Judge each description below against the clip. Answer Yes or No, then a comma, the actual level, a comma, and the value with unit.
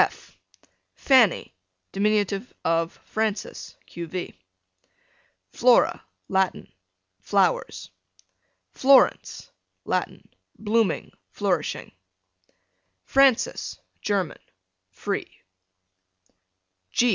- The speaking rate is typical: No, slow, 55 wpm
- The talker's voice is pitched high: Yes, high, 205 Hz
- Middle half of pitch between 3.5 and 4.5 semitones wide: Yes, average, 4.2 semitones